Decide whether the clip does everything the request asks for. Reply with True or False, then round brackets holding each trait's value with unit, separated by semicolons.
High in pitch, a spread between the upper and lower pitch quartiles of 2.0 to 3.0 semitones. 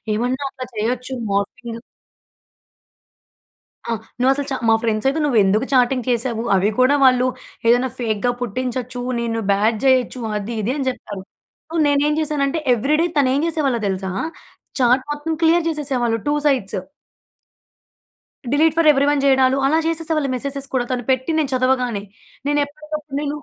False (260 Hz; 3.4 semitones)